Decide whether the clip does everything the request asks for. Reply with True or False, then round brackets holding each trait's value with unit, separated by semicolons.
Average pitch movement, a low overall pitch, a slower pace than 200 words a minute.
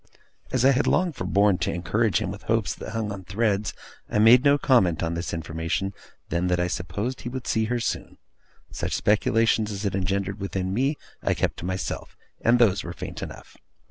False (4.0 semitones; 100 Hz; 205 wpm)